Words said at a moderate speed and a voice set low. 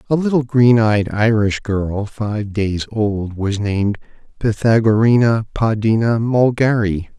No: slow, 115 wpm; low, 110 Hz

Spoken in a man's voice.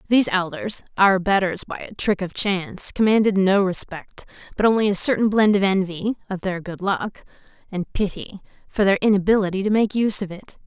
No: female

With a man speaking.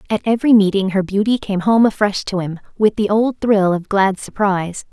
No: female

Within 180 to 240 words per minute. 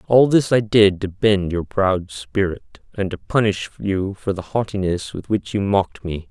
Yes: average, 200 wpm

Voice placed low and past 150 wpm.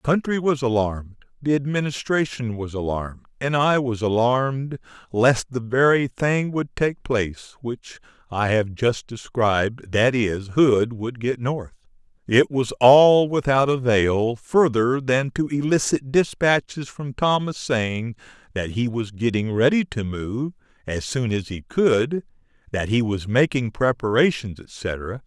No: low, 125 Hz; average, 145 wpm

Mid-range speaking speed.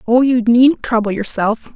Yes: average, 170 wpm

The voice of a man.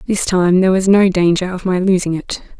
No: female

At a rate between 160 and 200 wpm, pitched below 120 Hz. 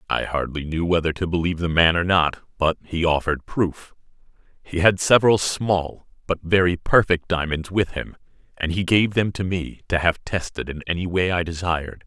Yes: average, 190 wpm; very low, 85 Hz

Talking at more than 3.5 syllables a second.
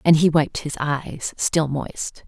No: 3.3 syllables/s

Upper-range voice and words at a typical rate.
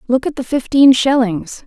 Yes: very high, 255 Hz; average, 180 wpm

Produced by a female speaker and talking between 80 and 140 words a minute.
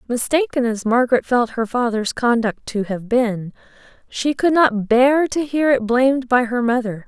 No: female; average, 180 wpm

